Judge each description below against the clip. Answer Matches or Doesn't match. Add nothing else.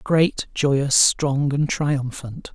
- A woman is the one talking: Doesn't match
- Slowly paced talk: Matches